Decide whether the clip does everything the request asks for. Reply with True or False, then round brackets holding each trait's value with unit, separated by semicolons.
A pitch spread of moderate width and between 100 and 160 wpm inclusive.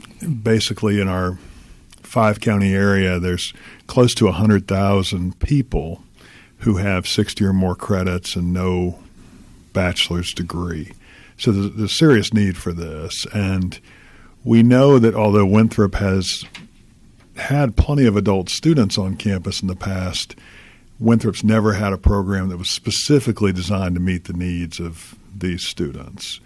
True (3.4 semitones; 140 wpm)